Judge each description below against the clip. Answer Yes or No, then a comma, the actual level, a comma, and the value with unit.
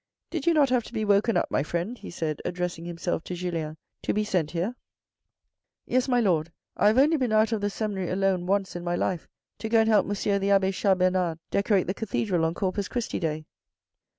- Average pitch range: Yes, average, 3.8 semitones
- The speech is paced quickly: Yes, fast, 235 wpm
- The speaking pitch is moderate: No, high, 195 Hz